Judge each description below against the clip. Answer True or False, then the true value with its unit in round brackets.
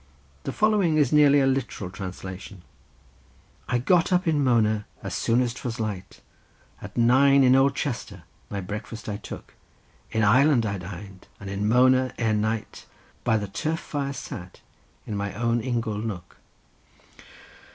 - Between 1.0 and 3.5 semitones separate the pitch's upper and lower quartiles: False (4.8 semitones)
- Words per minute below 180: True (150 wpm)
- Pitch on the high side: False (115 Hz)